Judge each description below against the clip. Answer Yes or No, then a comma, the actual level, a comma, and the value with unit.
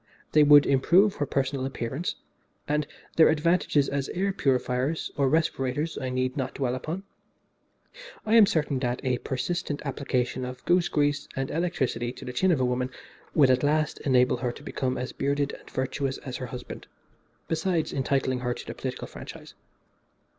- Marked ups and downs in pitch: No, average, 3.3 semitones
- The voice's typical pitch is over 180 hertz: No, medium, 140 Hz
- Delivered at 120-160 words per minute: No, average, 170 wpm